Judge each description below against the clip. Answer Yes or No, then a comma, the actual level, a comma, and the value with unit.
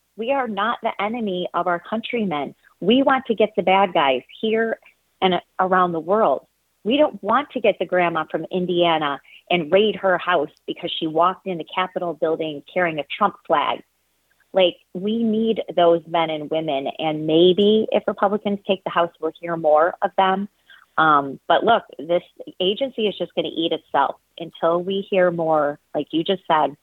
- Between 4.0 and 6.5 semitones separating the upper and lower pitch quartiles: No, average, 3.6 semitones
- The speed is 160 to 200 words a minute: Yes, average, 185 wpm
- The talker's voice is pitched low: No, medium, 185 Hz